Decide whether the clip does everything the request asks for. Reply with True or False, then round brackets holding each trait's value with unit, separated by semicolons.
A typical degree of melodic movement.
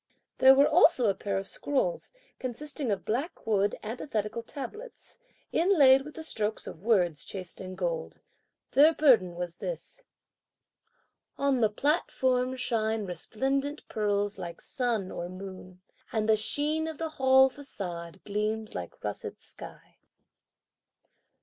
False (6.1 semitones)